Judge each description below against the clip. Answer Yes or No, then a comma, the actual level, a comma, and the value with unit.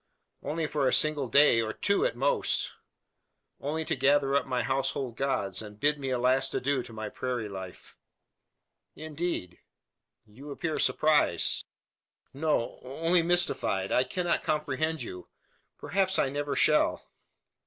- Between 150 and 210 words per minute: No, slow, 135 wpm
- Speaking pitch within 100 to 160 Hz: Yes, medium, 140 Hz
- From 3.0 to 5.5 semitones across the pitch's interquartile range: Yes, average, 3.8 semitones